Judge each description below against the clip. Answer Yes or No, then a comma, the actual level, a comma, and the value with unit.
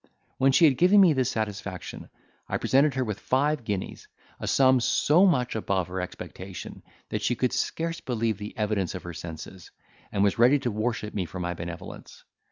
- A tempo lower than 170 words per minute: No, average, 185 wpm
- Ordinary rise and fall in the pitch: No, wide, 5.8 semitones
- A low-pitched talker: Yes, low, 110 Hz